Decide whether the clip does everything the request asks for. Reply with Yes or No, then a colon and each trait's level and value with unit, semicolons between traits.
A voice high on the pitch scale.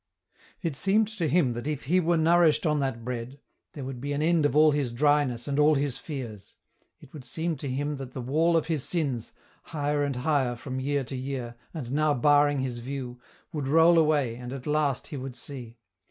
No: medium, 145 Hz